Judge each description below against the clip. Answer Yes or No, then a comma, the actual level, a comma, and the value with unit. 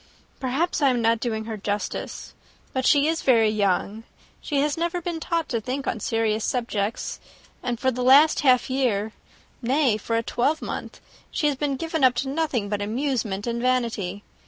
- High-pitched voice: Yes, very high, 250 Hz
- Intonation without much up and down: No, average, 4.4 semitones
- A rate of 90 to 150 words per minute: No, average, 180 wpm